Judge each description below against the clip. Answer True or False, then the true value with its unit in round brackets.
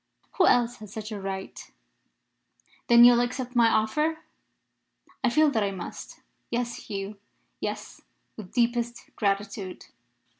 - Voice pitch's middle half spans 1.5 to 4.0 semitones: True (3.2 semitones)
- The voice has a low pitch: False (235 Hz)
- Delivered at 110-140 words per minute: True (135 wpm)